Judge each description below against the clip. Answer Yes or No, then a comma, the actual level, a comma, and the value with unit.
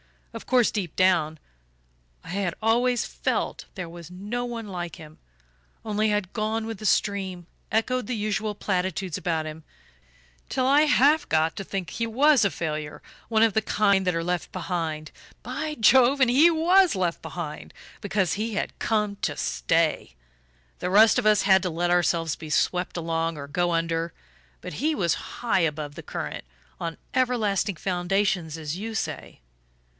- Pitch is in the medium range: No, high, 195 Hz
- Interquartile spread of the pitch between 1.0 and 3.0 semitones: No, average, 5.0 semitones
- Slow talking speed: No, average, 170 wpm